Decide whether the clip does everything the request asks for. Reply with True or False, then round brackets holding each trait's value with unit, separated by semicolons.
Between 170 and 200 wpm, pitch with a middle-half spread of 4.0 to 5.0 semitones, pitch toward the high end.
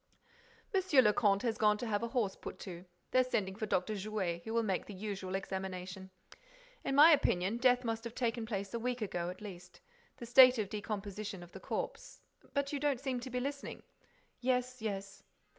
True (195 wpm; 4.4 semitones; 215 Hz)